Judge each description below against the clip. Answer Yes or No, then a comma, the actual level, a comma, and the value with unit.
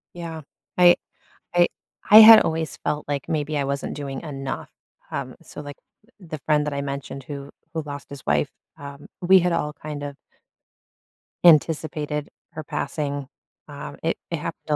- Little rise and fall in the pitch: Yes, narrow, 2.3 semitones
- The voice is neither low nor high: Yes, medium, 150 Hz